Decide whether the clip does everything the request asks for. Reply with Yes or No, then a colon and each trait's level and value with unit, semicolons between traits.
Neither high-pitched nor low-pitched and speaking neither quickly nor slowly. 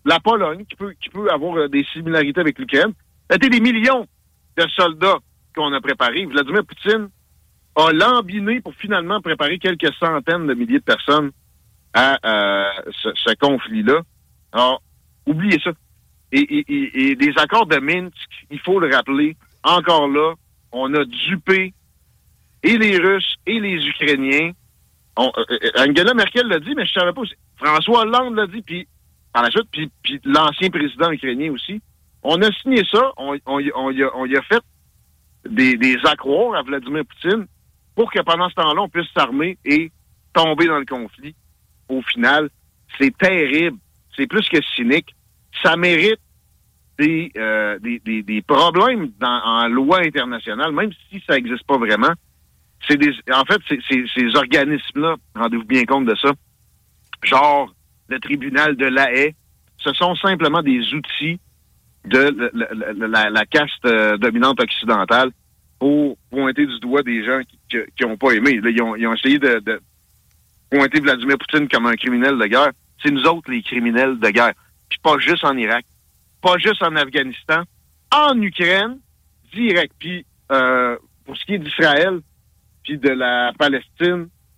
Yes: medium, 150 Hz; average, 165 wpm